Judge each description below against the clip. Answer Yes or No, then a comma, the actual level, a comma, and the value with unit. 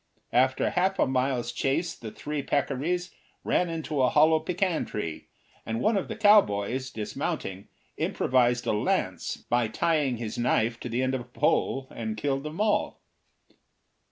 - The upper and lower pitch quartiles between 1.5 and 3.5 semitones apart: No, average, 5.3 semitones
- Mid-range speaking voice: No, low, 130 Hz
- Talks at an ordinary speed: Yes, average, 155 wpm